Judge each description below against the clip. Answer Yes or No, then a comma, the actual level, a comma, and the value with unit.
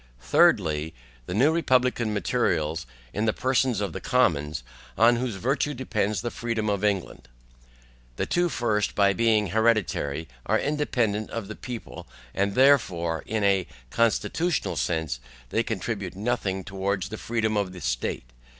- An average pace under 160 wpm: Yes, average, 140 wpm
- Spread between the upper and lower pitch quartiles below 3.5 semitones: No, average, 4.1 semitones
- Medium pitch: No, low, 105 Hz